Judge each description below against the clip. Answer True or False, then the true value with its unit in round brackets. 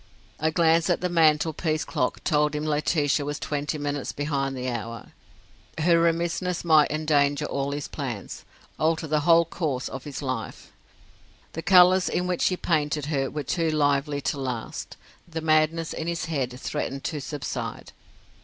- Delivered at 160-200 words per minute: True (165 wpm)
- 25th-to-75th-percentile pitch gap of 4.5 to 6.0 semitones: False (2.7 semitones)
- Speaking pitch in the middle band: True (150 Hz)